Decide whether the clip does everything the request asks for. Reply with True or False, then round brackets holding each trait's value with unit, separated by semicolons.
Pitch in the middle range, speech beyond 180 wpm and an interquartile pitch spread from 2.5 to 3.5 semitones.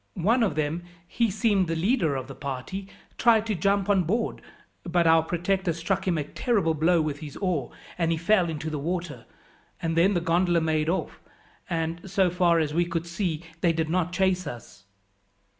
True (170 Hz; 190 wpm; 3.0 semitones)